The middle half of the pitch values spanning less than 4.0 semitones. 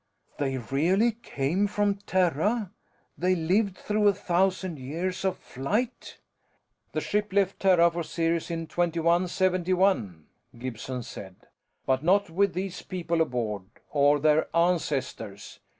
No: average, 4.9 semitones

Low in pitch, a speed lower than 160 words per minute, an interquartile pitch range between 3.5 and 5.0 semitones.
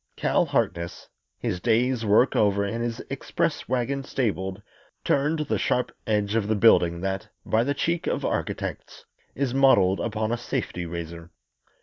Yes: low, 110 Hz; average, 150 wpm; average, 4.7 semitones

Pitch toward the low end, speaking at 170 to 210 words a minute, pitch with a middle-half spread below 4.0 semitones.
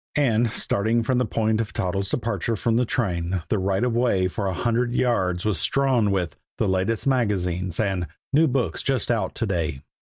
No: low, 110 Hz; average, 190 wpm; average, 4.3 semitones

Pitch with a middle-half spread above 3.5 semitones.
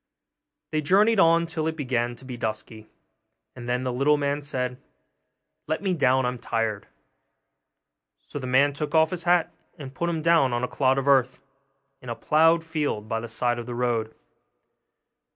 Yes: average, 4.7 semitones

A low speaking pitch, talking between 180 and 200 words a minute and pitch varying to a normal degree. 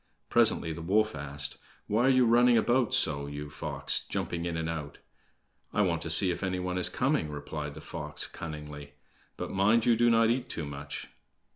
No: very low, 85 Hz; average, 190 wpm; wide, 6.8 semitones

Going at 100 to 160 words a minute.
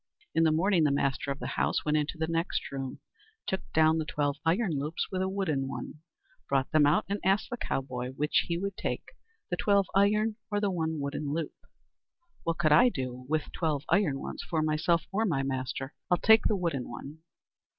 No: fast, 205 wpm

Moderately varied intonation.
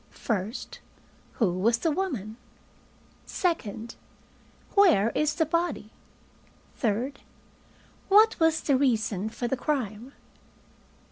No: wide, 6.9 semitones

